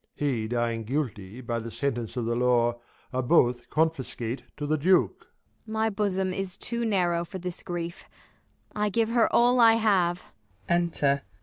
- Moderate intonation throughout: No, wide, 8.0 semitones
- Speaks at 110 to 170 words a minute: No, average, 185 wpm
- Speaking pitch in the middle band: Yes, medium, 160 Hz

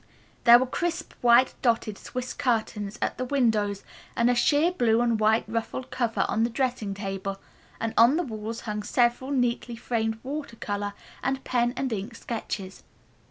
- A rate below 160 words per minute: No, average, 165 wpm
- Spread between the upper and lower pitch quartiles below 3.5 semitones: Yes, average, 2.7 semitones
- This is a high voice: Yes, high, 235 Hz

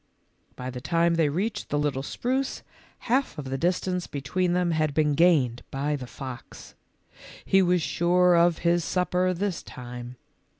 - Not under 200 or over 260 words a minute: No, average, 160 wpm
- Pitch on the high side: No, medium, 170 Hz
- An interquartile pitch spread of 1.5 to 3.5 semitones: No, average, 4.6 semitones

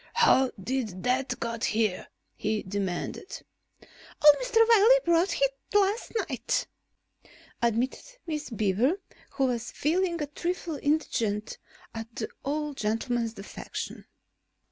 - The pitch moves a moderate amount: No, wide, 6.5 semitones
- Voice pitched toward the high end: Yes, very high, 260 Hz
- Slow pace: Yes, slow, 115 wpm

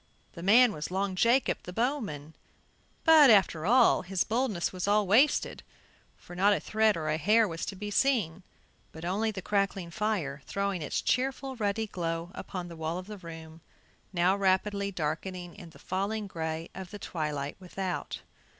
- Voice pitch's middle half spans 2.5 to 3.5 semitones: No, average, 4.1 semitones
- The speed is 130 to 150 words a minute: No, average, 170 wpm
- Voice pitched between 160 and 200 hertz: Yes, high, 190 Hz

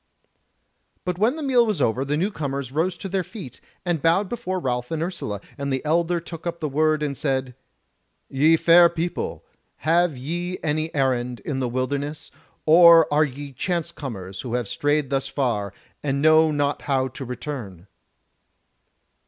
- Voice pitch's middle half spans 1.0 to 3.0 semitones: No, average, 4.3 semitones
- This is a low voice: No, medium, 150 Hz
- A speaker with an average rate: Yes, average, 170 wpm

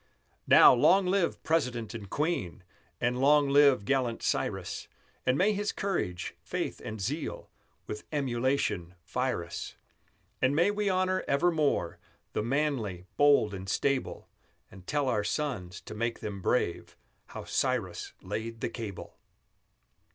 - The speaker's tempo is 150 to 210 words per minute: No, slow, 135 wpm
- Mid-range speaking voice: No, low, 130 Hz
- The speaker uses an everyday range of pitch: No, wide, 6.1 semitones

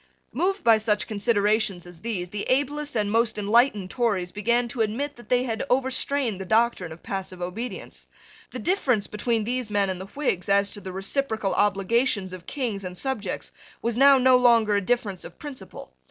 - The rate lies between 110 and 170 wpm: No, average, 185 wpm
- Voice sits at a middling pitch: No, high, 220 Hz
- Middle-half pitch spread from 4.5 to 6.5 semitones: No, average, 4.0 semitones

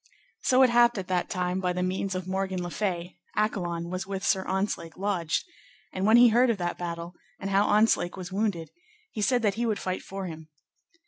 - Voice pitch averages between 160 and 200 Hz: Yes, high, 190 Hz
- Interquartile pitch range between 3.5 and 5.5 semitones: No, average, 2.9 semitones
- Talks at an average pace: No, fast, 210 wpm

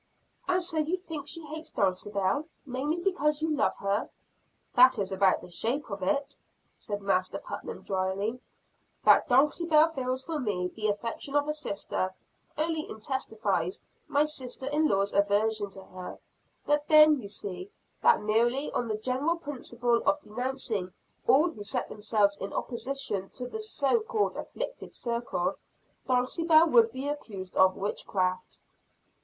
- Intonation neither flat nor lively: No, wide, 6.9 semitones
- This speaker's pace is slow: No, average, 150 wpm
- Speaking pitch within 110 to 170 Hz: No, very high, 250 Hz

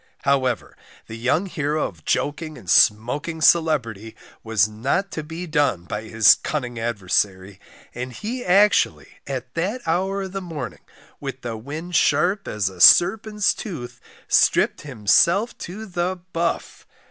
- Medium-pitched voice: Yes, medium, 145 Hz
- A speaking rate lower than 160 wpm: Yes, average, 140 wpm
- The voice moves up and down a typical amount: No, wide, 7.9 semitones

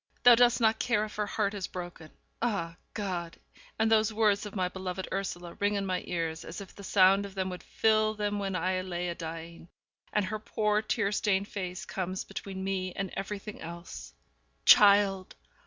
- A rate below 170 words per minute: No, average, 190 wpm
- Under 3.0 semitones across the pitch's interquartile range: Yes, narrow, 2.5 semitones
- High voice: Yes, high, 195 Hz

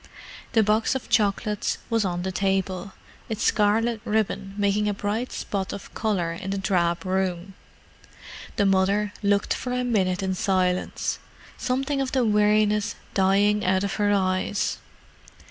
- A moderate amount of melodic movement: No, narrow, 2.0 semitones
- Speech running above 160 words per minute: No, average, 145 wpm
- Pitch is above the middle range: Yes, high, 200 Hz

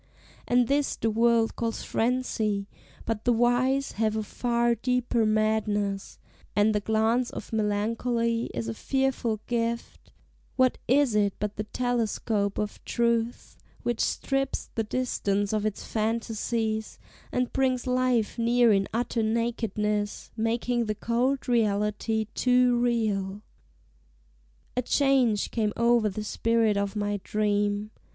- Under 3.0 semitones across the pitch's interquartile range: Yes, narrow, 2.4 semitones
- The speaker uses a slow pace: Yes, slow, 130 wpm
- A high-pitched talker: Yes, high, 225 Hz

